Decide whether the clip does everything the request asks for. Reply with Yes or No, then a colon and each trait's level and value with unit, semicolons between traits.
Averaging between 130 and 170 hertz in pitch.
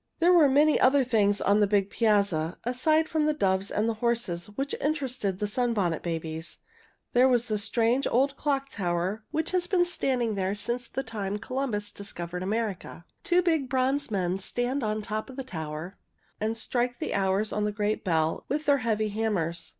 No: high, 220 Hz